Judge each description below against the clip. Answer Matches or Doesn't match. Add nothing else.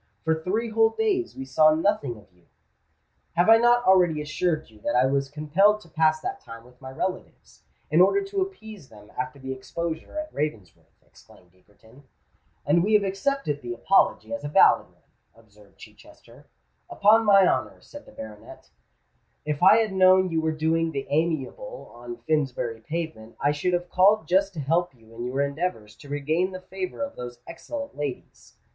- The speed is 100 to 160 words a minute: Doesn't match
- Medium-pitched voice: Matches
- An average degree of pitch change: Doesn't match